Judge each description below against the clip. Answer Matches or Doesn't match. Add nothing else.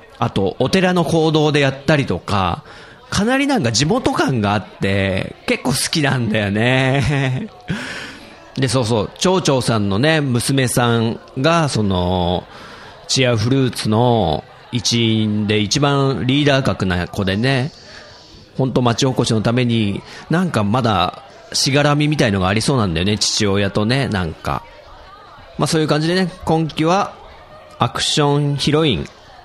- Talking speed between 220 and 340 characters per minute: Matches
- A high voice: Doesn't match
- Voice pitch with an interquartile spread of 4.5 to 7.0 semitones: Matches